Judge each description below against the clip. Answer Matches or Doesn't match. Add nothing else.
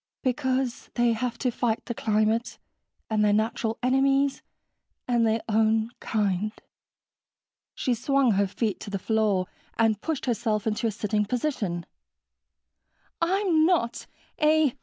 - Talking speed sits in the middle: Doesn't match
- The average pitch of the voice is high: Matches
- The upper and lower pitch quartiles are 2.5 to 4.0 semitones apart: Matches